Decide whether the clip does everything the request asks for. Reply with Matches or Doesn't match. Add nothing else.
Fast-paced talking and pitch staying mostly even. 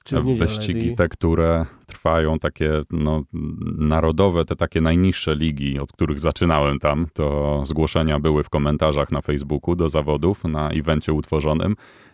Doesn't match